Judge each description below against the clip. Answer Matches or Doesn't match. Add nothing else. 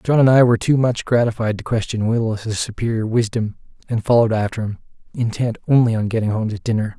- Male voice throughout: Matches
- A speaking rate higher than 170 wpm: Matches